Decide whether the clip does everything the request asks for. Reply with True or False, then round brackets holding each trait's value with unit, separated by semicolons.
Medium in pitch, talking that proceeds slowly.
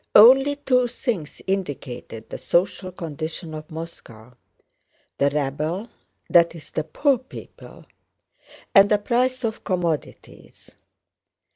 True (175 Hz; 105 wpm)